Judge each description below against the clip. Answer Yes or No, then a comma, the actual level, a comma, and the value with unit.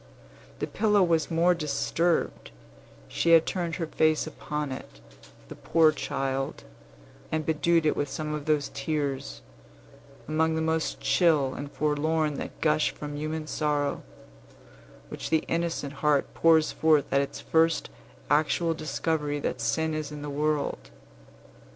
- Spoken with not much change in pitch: Yes, narrow, 1.8 semitones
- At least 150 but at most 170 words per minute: No, average, 140 wpm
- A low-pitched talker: No, medium, 155 Hz